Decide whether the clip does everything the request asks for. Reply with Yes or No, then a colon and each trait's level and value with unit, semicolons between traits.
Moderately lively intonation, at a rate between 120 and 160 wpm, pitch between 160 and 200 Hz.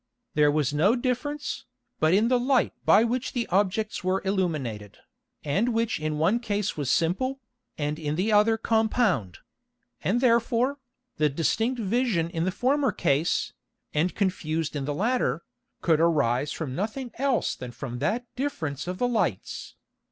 No: wide, 7.6 semitones; average, 155 wpm; high, 190 Hz